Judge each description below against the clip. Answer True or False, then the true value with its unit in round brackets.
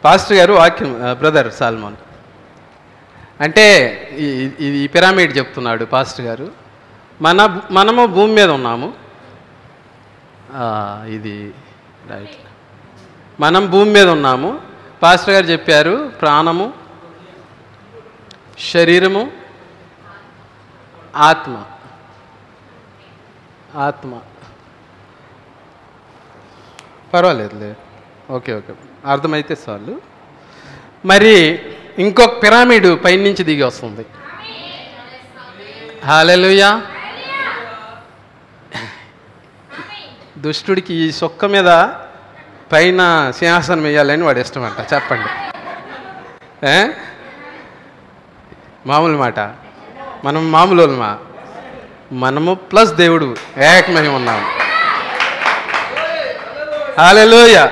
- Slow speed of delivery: True (65 wpm)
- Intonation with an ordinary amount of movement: False (7.2 semitones)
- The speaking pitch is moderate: True (150 Hz)